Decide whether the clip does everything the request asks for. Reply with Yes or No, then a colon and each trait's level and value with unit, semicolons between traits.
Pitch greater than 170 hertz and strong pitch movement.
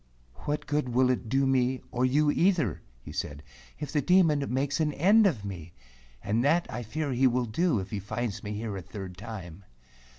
No: low, 125 Hz; wide, 6.0 semitones